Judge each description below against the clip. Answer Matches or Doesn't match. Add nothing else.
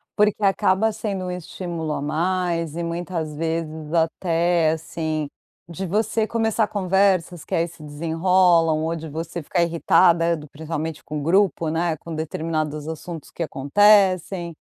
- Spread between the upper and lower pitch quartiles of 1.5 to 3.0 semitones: Matches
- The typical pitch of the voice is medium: Matches